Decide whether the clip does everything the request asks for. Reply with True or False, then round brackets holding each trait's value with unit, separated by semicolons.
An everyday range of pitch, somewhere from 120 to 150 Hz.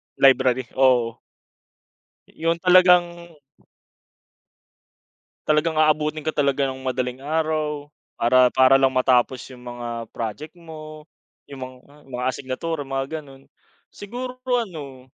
True (3.6 semitones; 140 Hz)